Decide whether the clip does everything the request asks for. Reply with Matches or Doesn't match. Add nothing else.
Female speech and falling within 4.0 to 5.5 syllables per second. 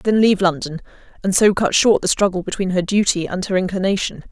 Doesn't match